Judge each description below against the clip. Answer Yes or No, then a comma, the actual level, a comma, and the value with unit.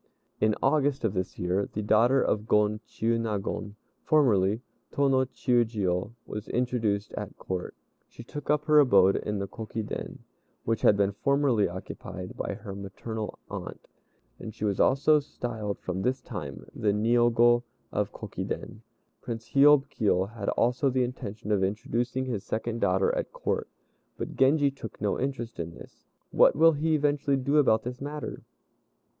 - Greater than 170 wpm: No, average, 155 wpm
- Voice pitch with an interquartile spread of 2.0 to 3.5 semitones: No, average, 4.7 semitones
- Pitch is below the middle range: Yes, low, 115 Hz